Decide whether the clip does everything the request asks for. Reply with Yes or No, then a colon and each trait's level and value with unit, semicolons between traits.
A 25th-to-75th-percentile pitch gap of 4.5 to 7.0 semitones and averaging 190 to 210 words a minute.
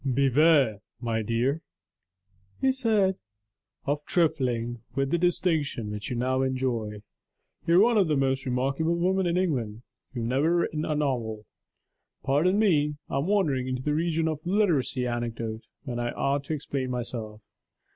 No: wide, 5.4 semitones; average, 155 wpm